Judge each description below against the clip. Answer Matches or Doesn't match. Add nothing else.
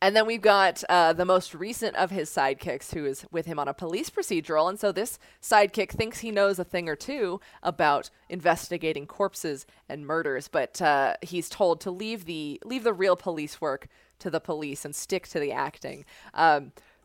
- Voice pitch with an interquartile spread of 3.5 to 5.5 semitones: Matches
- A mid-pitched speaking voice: Matches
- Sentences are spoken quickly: Doesn't match